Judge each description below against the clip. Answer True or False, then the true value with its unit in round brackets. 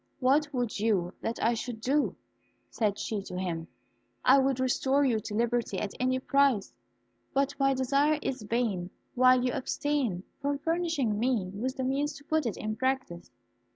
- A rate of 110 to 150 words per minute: False (170 wpm)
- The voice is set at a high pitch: True (255 Hz)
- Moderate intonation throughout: True (4.3 semitones)